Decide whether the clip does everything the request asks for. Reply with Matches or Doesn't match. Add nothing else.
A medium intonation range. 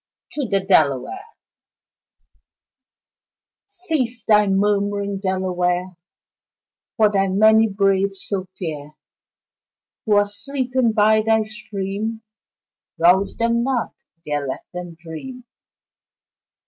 Matches